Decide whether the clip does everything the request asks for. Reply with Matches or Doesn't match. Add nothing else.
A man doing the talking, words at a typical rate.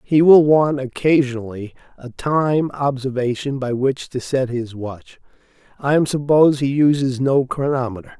Matches